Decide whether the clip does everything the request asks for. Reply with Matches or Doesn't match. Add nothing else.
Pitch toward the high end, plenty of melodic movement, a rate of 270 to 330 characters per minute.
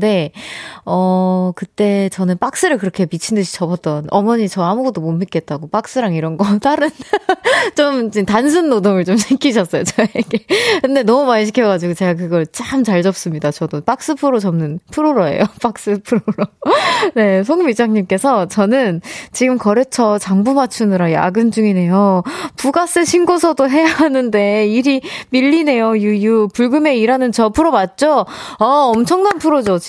Matches